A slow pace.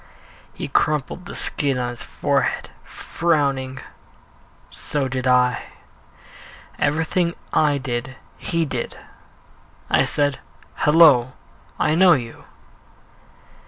Yes: slow, 95 wpm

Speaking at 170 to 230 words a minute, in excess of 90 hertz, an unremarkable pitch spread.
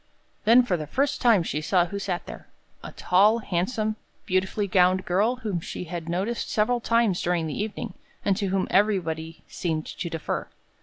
Yes: average, 175 wpm; high, 190 Hz; average, 3.8 semitones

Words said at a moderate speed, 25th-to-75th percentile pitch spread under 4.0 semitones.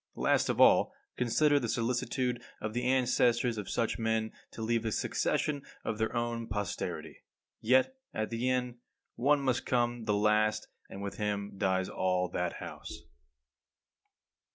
Yes: average, 150 wpm; narrow, 2.6 semitones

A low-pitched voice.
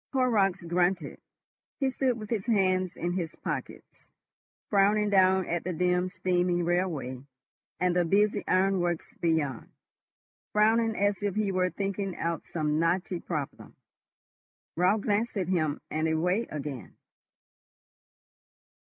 No: medium, 185 Hz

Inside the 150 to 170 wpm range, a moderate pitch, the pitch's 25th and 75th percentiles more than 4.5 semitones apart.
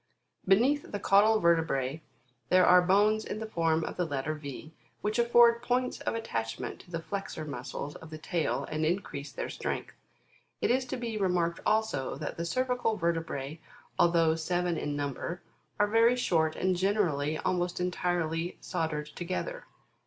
Yes: average, 160 wpm; medium, 175 Hz; average, 5.2 semitones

